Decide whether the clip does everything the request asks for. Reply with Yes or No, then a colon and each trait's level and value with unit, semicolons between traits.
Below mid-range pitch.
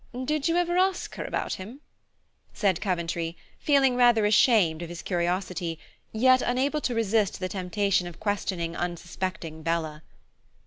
No: high, 195 Hz